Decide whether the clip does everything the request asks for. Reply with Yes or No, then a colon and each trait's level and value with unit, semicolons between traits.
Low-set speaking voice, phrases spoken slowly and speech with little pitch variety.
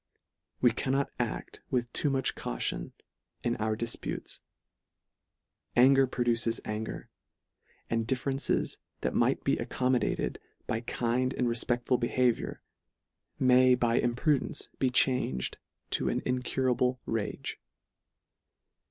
Yes: low, 125 Hz; slow, 105 wpm; narrow, 1.6 semitones